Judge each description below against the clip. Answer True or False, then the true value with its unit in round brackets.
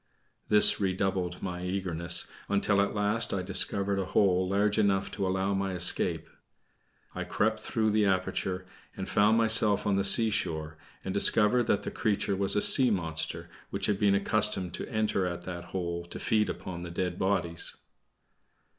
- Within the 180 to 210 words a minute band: False (165 wpm)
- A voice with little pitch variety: True (2.3 semitones)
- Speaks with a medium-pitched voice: False (95 Hz)